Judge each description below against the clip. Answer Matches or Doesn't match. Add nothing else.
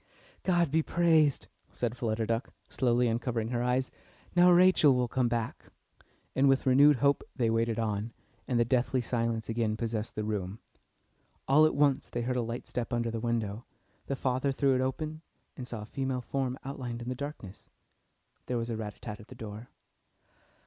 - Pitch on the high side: Doesn't match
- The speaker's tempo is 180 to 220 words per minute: Matches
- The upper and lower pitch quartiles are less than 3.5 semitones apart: Matches